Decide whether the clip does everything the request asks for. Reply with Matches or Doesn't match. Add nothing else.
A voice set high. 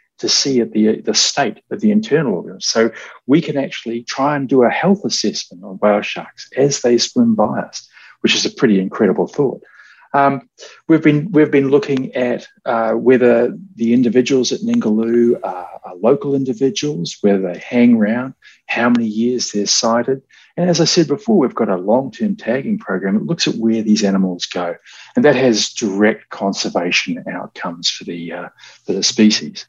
Doesn't match